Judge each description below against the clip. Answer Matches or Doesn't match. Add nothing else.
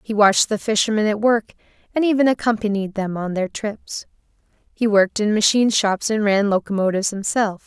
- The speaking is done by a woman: Matches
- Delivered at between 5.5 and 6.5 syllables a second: Matches